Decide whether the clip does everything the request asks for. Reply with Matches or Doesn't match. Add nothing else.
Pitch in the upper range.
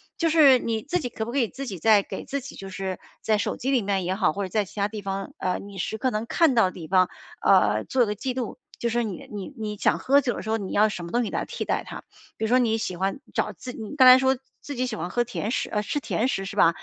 Matches